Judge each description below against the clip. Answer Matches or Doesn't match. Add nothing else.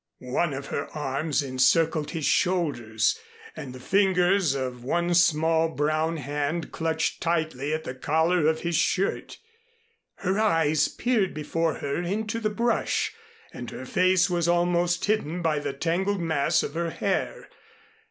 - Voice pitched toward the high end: Doesn't match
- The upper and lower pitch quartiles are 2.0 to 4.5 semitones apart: Matches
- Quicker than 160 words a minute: Doesn't match